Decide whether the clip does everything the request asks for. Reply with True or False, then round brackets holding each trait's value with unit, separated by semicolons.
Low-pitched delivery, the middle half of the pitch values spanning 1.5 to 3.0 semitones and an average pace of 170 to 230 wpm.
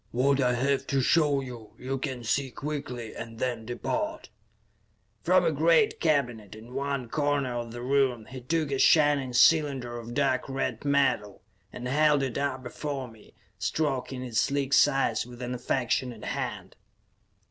False (130 Hz; 2.7 semitones; 160 wpm)